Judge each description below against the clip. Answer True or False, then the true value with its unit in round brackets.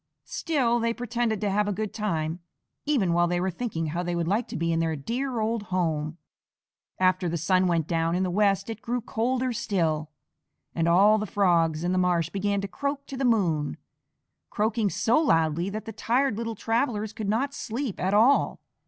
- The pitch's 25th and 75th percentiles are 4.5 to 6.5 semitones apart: True (5.1 semitones)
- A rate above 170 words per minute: True (195 wpm)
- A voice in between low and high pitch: False (200 Hz)